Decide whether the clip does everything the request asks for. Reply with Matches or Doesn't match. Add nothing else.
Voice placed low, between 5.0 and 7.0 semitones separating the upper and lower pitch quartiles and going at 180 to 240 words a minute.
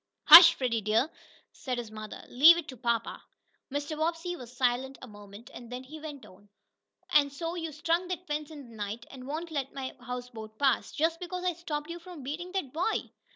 Doesn't match